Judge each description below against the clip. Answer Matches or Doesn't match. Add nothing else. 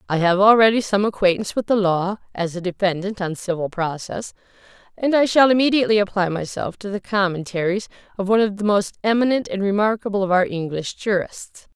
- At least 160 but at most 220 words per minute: Matches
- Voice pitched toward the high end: Matches